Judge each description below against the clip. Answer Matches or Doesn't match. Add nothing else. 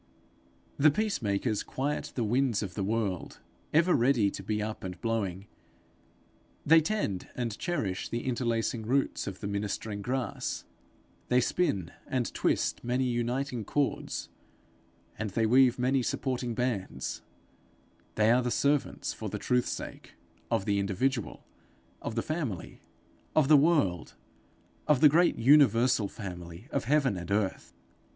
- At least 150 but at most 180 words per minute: Doesn't match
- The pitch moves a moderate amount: Matches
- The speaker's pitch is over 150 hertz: Doesn't match